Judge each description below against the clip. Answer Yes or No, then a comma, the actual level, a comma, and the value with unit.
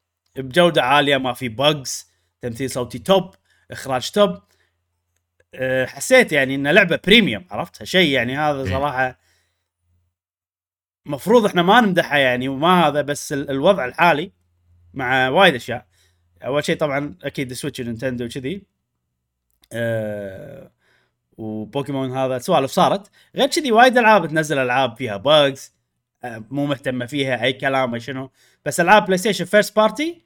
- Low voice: Yes, low, 130 Hz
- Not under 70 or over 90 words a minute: No, average, 130 wpm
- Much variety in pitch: Yes, wide, 6.7 semitones